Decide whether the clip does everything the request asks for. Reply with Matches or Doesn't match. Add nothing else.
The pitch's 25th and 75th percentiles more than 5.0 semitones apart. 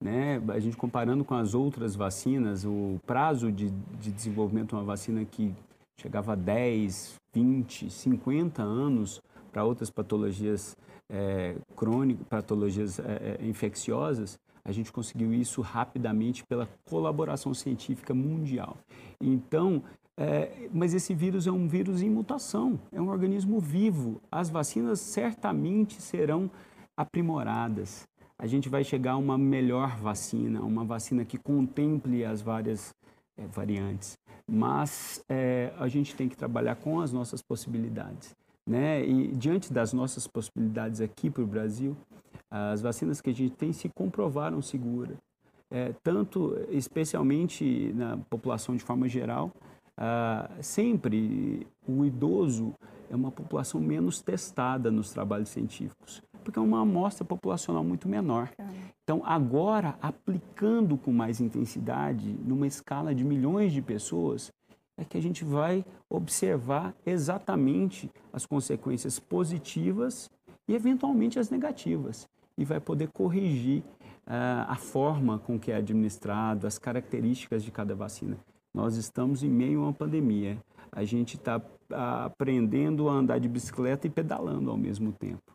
Matches